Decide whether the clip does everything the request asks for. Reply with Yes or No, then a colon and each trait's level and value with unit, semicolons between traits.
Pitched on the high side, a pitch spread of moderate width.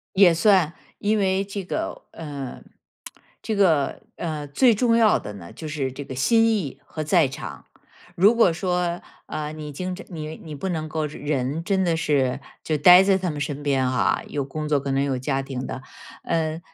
No: medium, 155 Hz; average, 4.7 semitones